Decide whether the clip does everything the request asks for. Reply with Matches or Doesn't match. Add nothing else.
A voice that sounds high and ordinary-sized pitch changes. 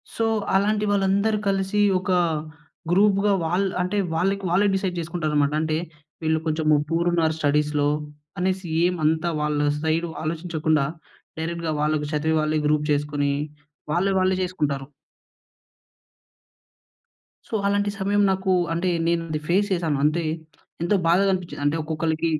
Doesn't match